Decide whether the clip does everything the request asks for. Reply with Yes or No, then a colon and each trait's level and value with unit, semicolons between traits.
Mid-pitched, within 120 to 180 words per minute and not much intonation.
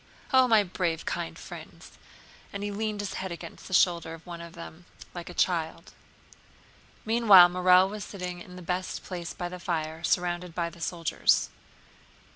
Yes: medium, 180 Hz; average, 175 wpm; narrow, 2.0 semitones